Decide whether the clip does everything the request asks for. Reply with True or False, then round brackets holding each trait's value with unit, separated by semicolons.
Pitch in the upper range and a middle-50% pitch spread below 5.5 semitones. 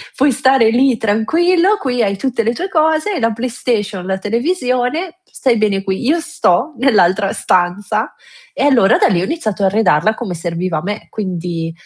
False (225 Hz; 6.0 semitones)